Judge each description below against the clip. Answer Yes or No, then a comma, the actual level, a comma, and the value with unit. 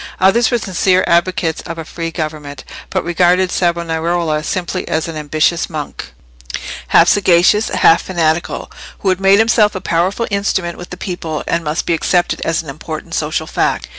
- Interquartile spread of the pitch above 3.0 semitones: No, average, 2.7 semitones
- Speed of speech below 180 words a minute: Yes, average, 160 wpm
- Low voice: No, medium, 170 Hz